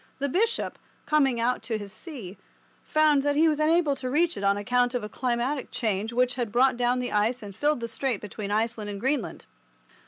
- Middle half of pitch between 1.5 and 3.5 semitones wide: No, average, 4.9 semitones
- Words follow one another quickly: Yes, fast, 210 wpm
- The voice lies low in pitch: No, high, 245 Hz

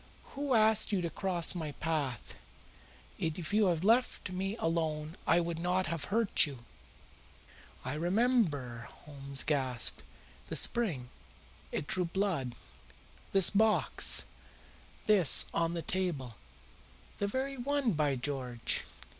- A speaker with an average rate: No, slow, 120 wpm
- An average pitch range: No, wide, 5.9 semitones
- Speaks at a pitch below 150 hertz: No, medium, 170 Hz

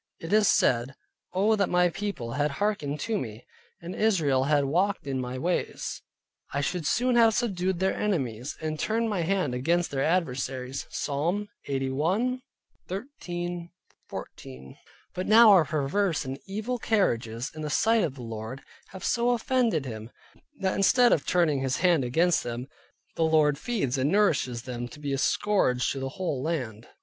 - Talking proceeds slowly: No, average, 165 wpm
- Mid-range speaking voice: Yes, medium, 160 Hz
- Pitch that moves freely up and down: Yes, wide, 7.0 semitones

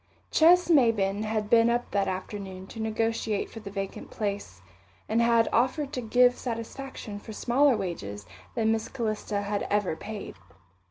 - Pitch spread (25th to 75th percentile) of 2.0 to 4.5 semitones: Yes, average, 2.8 semitones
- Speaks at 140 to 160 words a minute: Yes, average, 155 wpm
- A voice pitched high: Yes, high, 220 Hz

